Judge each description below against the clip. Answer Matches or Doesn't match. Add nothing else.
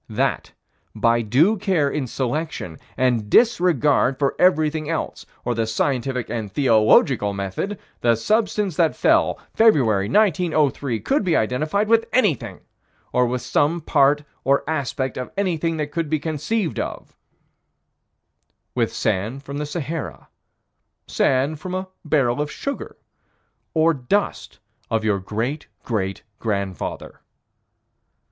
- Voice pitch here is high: Doesn't match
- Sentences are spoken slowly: Matches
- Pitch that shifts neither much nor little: Doesn't match